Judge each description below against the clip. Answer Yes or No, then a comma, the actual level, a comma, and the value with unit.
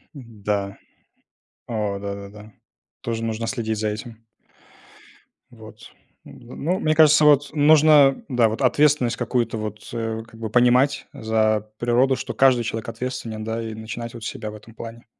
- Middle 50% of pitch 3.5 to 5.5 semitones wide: No, average, 2.9 semitones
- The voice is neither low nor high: No, low, 115 Hz